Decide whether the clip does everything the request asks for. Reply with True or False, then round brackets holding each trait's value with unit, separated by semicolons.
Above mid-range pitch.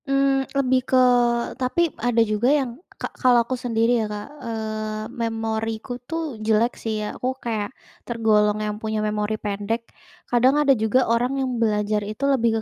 True (230 Hz)